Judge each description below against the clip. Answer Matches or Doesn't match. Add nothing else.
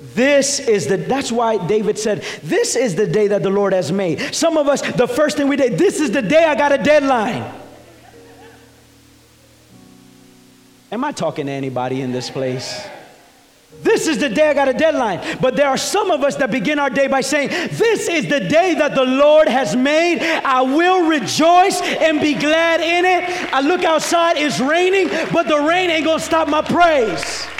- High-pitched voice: Matches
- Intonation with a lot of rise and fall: Matches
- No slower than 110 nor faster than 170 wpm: Doesn't match